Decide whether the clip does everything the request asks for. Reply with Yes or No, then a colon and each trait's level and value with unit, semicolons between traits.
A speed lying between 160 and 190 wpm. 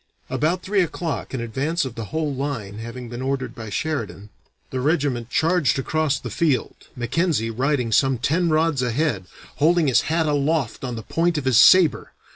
Yes: average, 175 wpm